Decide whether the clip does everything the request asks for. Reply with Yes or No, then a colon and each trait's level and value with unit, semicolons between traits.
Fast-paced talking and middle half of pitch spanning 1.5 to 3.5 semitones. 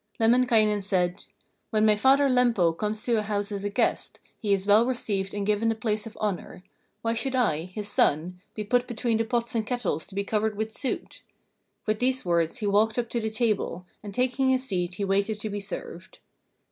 Yes: fast, 210 wpm; average, 2.9 semitones